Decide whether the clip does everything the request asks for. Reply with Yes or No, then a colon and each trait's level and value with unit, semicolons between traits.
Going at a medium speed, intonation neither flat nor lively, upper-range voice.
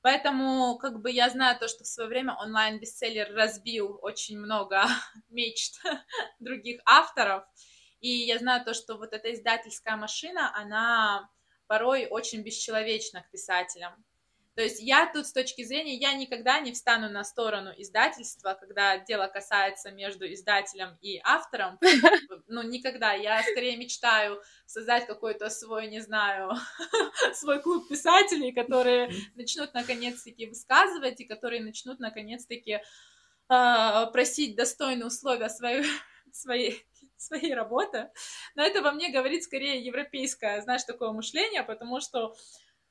Yes: average, 130 wpm; average, 3.2 semitones; high, 235 Hz